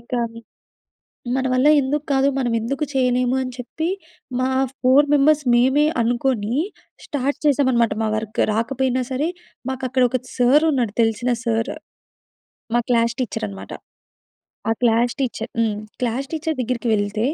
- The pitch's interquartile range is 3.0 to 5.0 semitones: No, narrow, 2.5 semitones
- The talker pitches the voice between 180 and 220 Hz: No, very high, 250 Hz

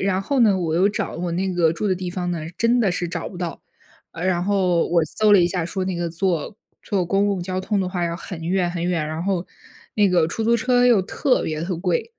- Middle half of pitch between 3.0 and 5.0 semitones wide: No, narrow, 2.5 semitones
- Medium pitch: Yes, medium, 180 Hz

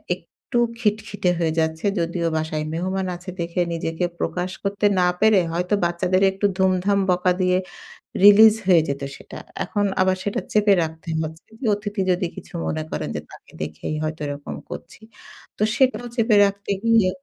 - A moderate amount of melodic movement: Yes, average, 3.4 semitones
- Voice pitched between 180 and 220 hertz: Yes, medium, 185 Hz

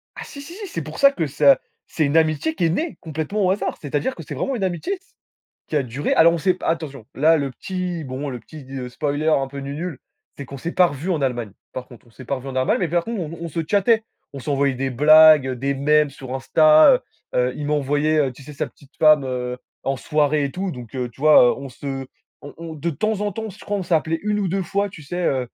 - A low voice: No, medium, 150 Hz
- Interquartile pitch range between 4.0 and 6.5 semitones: Yes, average, 4.4 semitones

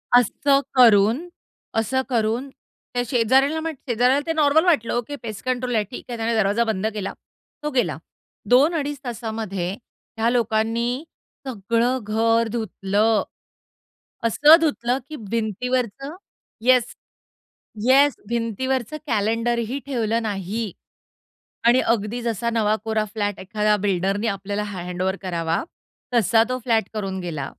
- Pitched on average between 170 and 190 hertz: No, high, 230 Hz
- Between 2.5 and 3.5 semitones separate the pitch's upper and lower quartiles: Yes, average, 3.2 semitones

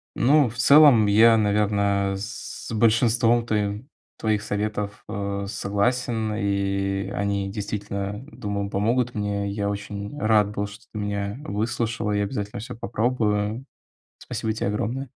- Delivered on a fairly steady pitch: Yes, narrow, 2.2 semitones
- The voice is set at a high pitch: No, low, 105 Hz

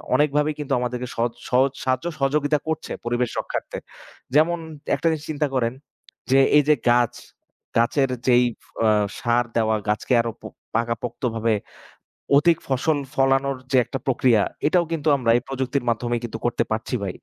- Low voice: Yes, low, 125 Hz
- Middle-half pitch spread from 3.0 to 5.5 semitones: Yes, average, 3.4 semitones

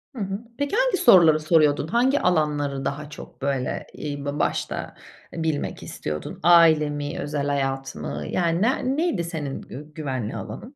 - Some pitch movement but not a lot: Yes, average, 3.9 semitones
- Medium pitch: Yes, medium, 150 Hz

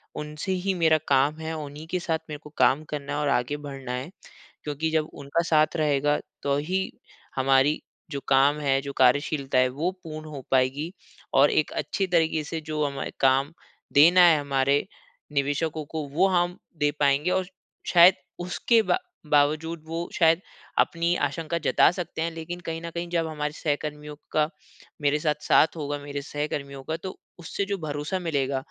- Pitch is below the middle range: No, medium, 150 Hz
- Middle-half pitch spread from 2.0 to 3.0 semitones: Yes, average, 2.7 semitones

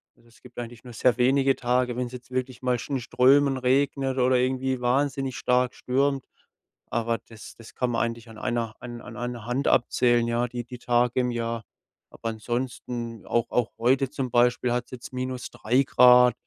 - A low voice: Yes, low, 125 Hz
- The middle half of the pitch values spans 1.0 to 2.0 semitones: Yes, narrow, 1.4 semitones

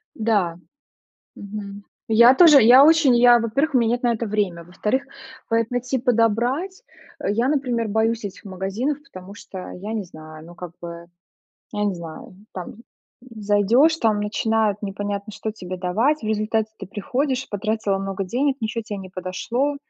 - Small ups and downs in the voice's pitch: No, average, 3.9 semitones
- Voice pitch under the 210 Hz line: No, high, 220 Hz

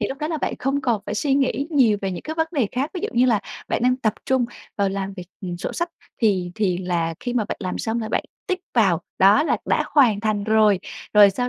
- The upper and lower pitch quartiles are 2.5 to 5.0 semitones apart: No, wide, 5.4 semitones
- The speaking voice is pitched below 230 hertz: Yes, high, 220 Hz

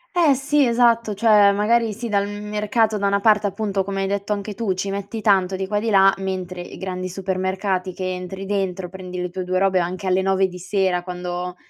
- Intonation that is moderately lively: No, narrow, 2.1 semitones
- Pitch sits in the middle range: No, high, 195 Hz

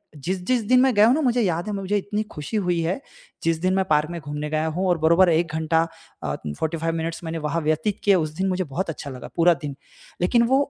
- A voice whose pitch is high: No, medium, 170 Hz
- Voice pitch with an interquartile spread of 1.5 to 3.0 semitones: No, average, 3.5 semitones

